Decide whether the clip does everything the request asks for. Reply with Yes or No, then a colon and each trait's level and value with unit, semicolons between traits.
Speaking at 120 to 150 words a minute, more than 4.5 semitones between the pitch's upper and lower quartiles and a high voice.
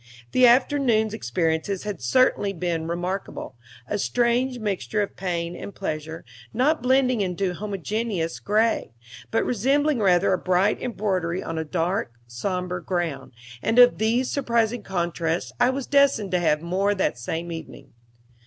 Yes: average, 145 wpm; wide, 5.5 semitones; high, 195 Hz